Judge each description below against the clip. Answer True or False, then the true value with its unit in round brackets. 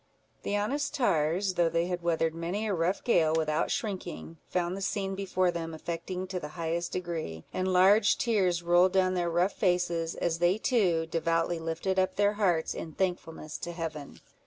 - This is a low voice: False (175 Hz)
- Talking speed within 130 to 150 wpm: False (180 wpm)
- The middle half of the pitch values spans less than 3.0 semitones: True (2.5 semitones)